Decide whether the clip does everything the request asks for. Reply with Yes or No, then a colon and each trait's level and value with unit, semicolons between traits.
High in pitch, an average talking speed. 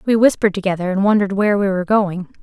No: high, 200 Hz; fast, 225 wpm